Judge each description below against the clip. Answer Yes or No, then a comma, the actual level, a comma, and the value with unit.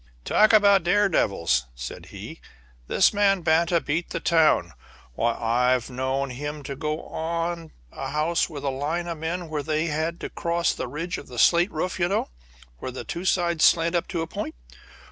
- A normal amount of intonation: Yes, average, 3.8 semitones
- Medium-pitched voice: Yes, medium, 160 Hz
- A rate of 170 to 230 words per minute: Yes, average, 190 wpm